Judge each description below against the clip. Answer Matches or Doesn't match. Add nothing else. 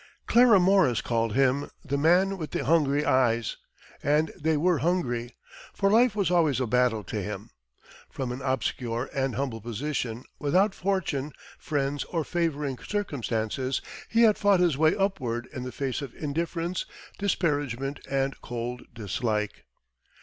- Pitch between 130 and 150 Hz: Matches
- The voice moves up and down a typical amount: Doesn't match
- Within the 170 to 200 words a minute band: Doesn't match